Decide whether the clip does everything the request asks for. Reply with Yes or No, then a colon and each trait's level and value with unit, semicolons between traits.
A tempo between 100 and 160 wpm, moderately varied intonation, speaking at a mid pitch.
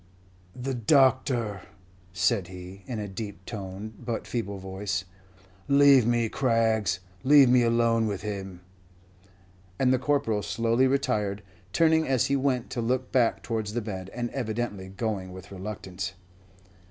No: average, 140 wpm; average, 4.4 semitones; low, 115 Hz